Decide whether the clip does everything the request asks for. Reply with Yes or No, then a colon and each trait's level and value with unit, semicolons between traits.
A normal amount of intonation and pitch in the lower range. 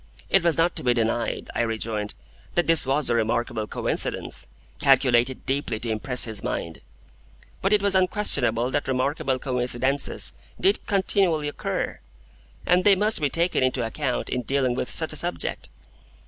No: wide, 6.0 semitones; low, 130 Hz